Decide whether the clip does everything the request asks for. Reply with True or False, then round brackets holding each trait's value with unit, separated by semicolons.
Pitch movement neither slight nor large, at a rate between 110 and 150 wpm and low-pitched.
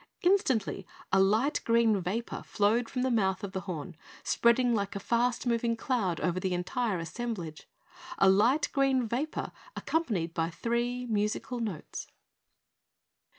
False (4.3 semitones; 140 wpm; 225 Hz)